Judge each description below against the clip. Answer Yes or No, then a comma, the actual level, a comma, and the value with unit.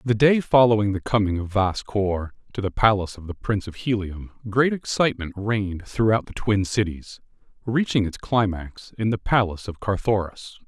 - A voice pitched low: Yes, low, 105 Hz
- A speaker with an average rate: Yes, average, 175 wpm